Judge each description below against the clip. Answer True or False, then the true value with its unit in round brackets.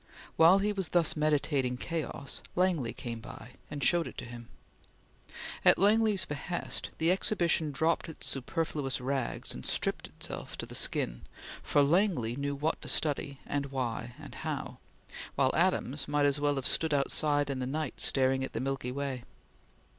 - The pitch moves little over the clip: False (3.7 semitones)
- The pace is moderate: True (165 wpm)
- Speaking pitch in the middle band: True (145 Hz)